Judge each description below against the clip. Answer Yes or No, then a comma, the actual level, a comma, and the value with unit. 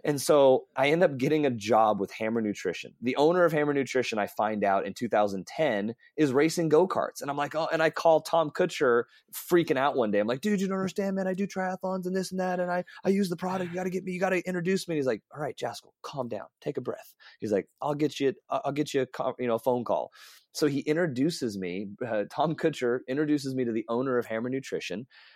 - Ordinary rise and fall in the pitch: No, wide, 6.5 semitones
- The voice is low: No, medium, 150 Hz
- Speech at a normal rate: No, fast, 255 wpm